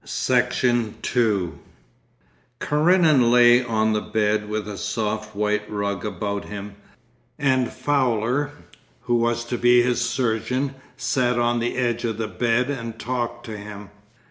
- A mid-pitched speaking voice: No, low, 120 Hz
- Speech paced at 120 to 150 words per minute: Yes, average, 140 wpm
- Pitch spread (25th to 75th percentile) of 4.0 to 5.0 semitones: No, average, 2.7 semitones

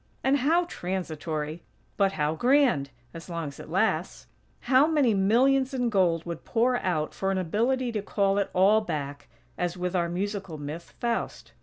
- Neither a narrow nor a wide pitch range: No, wide, 6.4 semitones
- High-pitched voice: Yes, high, 195 Hz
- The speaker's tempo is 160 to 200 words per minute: Yes, average, 170 wpm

